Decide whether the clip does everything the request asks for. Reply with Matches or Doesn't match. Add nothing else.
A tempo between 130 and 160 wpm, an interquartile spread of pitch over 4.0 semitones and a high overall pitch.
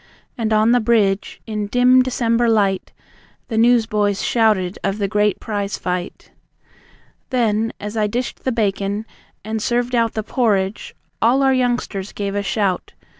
Doesn't match